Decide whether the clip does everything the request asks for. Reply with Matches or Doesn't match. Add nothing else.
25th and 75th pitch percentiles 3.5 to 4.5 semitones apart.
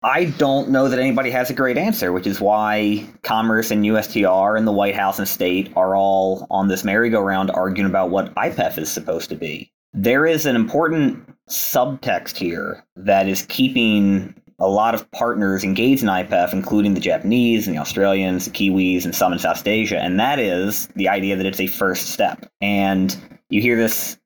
Doesn't match